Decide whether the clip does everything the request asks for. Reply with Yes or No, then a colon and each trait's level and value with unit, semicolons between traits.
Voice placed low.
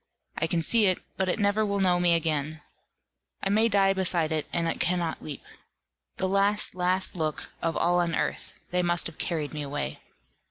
No: medium, 175 Hz